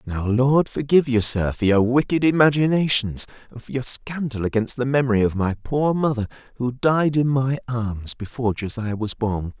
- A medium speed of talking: Yes, average, 180 wpm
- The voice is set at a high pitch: No, low, 125 Hz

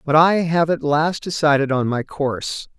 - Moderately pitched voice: Yes, medium, 155 Hz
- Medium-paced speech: Yes, average, 195 wpm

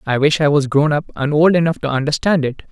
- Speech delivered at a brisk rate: Yes, fast, 265 wpm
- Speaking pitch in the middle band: Yes, medium, 150 Hz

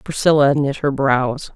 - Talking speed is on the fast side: No, average, 155 wpm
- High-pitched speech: No, medium, 140 Hz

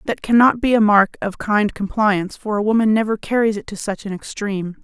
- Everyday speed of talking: No, fast, 225 wpm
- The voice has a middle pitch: No, high, 210 Hz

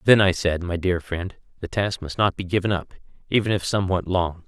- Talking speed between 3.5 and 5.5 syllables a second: No, 5.7 syllables/s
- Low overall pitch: Yes, very low, 90 Hz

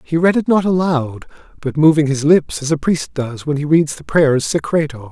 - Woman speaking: No, male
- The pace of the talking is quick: Yes, fast, 225 wpm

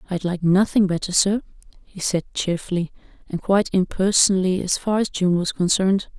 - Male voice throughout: No, female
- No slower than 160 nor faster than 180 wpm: Yes, average, 165 wpm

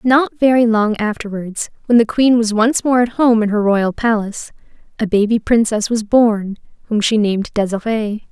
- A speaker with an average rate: Yes, average, 180 wpm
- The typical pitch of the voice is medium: No, high, 220 Hz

